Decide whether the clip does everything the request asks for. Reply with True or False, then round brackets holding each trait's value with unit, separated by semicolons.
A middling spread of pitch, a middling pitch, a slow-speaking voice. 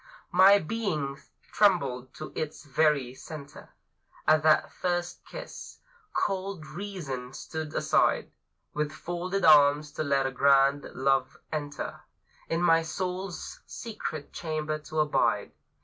True (3.7 semitones; 155 Hz; 115 wpm)